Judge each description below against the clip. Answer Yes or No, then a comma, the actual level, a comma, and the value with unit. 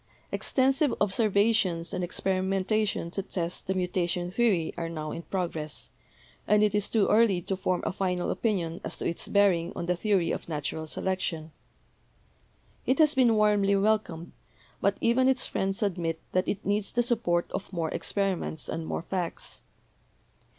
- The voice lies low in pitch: No, high, 190 Hz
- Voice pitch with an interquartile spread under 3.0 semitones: No, average, 3.5 semitones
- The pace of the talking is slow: No, average, 160 wpm